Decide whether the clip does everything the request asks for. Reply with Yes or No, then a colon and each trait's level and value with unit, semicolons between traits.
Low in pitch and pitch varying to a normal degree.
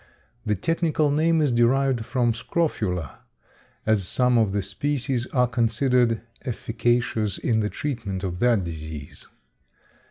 Yes: low, 120 Hz; average, 4.1 semitones